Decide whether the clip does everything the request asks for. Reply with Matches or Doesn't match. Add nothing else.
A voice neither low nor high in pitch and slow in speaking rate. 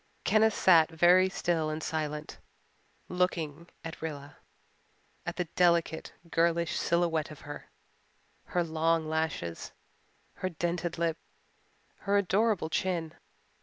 Matches